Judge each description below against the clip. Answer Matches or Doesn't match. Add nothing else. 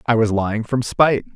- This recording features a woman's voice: Doesn't match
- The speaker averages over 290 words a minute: Doesn't match